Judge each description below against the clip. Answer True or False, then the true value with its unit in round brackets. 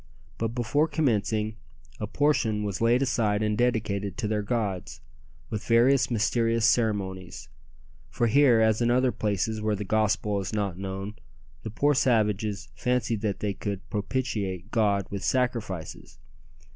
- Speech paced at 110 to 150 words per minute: True (145 wpm)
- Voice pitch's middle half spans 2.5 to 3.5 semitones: True (2.8 semitones)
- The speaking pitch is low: True (110 Hz)